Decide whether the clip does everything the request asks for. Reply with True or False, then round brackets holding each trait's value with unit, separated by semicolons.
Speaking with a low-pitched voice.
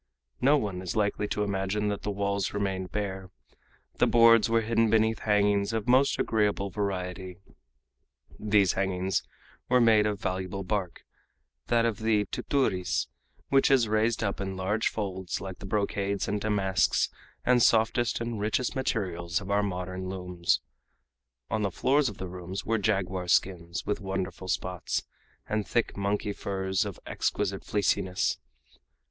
True (100 Hz)